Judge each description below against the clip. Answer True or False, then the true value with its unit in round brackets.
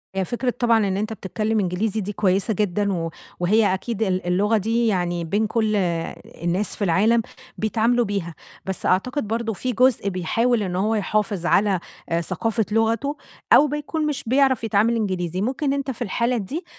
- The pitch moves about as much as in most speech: True (3.8 semitones)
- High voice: True (215 Hz)